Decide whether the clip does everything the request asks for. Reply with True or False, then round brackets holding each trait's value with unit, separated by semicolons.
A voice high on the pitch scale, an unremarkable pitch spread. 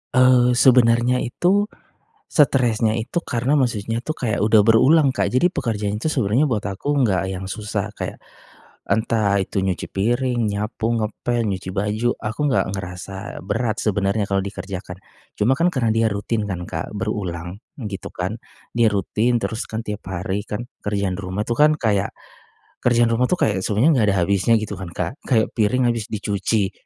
False (110 Hz; 3.2 semitones)